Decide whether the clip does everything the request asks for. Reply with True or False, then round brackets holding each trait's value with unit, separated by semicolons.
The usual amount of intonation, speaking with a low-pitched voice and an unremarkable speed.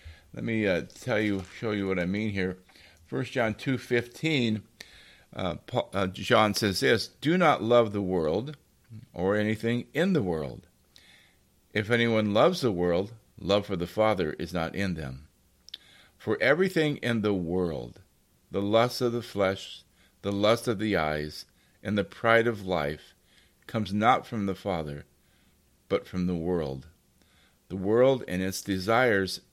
True (4.0 semitones; 100 Hz; 160 wpm)